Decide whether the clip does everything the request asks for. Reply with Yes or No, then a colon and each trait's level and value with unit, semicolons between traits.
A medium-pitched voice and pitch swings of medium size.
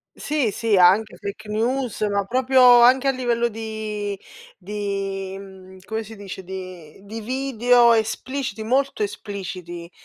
No: high, 215 Hz; average, 3.6 semitones